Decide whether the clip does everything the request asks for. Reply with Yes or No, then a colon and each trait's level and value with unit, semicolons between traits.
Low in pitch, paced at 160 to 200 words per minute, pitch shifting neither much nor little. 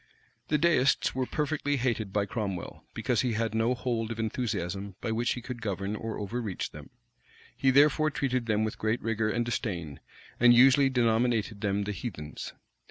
Yes: low, 115 Hz; average, 170 wpm; average, 3.3 semitones